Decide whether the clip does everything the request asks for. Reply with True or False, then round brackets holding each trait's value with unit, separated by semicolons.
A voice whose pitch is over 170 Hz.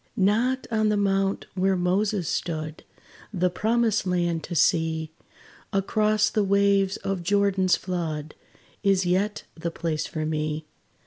True (190 Hz)